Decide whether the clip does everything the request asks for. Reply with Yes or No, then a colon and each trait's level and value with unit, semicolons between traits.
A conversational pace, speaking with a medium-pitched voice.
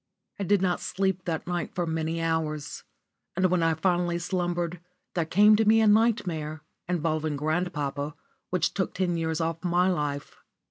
Yes: average, 170 wpm; medium, 175 Hz